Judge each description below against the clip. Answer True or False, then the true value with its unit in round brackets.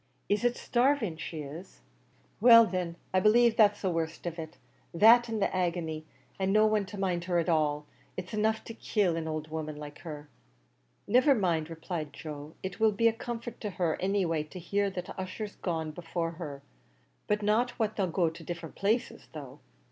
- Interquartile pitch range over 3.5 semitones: True (4.8 semitones)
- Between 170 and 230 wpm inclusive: True (195 wpm)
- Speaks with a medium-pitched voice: True (180 Hz)